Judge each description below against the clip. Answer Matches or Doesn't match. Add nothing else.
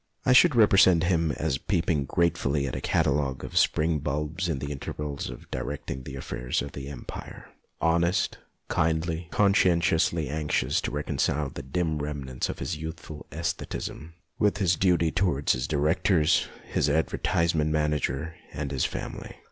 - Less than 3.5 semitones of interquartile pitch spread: Matches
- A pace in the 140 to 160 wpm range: Matches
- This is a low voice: Matches